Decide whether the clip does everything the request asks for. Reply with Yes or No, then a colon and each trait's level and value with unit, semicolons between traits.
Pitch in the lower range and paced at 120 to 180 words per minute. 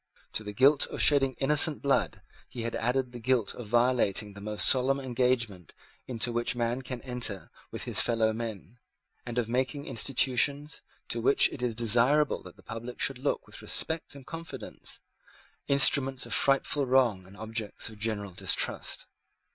Yes: low, 125 Hz; average, 165 wpm